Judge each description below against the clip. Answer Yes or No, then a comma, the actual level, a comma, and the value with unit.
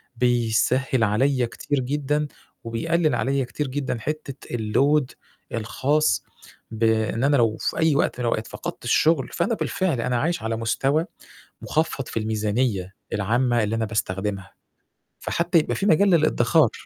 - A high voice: No, low, 125 Hz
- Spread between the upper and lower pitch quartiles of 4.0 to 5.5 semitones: Yes, average, 4.8 semitones